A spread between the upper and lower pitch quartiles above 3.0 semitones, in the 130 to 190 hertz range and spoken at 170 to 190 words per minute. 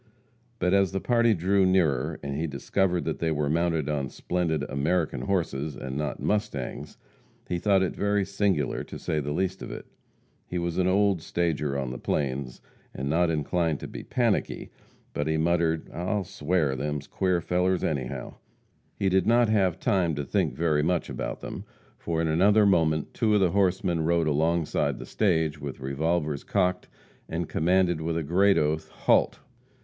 No: average, 3.8 semitones; very low, 85 Hz; average, 175 wpm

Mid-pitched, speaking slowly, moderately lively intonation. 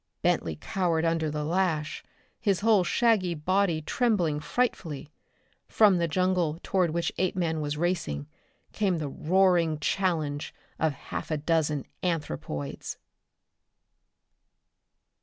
Yes: medium, 165 Hz; slow, 110 wpm; average, 3.6 semitones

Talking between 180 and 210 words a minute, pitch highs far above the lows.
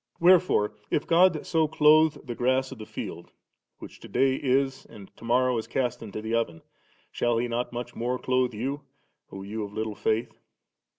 No: average, 185 wpm; average, 3.4 semitones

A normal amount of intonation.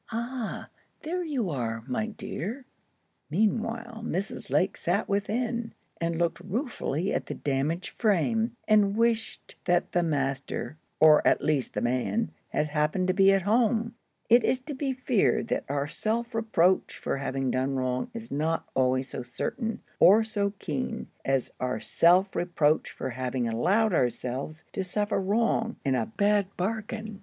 No: wide, 7.7 semitones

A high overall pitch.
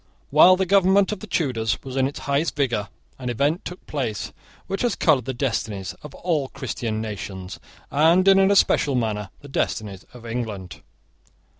No: low, 135 Hz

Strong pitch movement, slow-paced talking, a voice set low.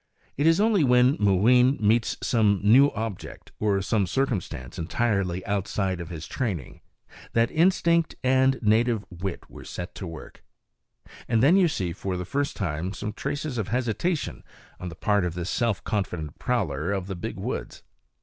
No: wide, 5.7 semitones; average, 165 wpm; low, 105 Hz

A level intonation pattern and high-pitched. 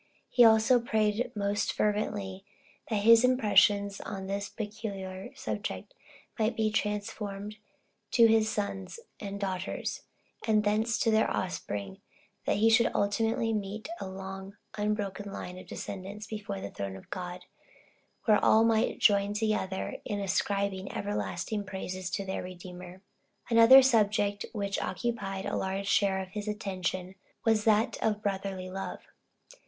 Yes: narrow, 2.3 semitones; high, 205 Hz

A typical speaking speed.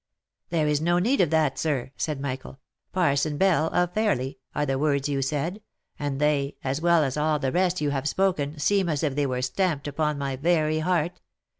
No: fast, 210 wpm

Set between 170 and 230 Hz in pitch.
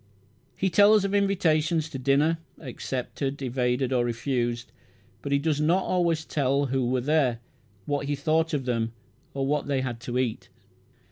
No: medium, 140 Hz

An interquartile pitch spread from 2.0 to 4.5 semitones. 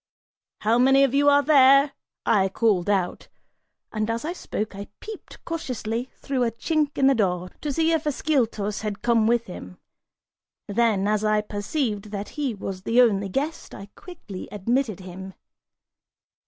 No: wide, 5.4 semitones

